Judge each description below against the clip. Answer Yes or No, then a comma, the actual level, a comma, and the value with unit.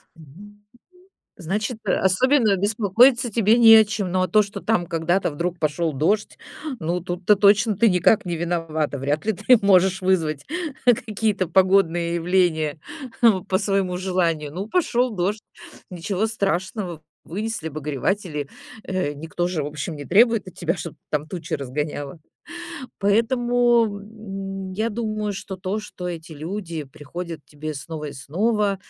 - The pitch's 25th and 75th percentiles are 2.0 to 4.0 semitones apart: No, average, 4.5 semitones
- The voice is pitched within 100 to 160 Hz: No, medium, 185 Hz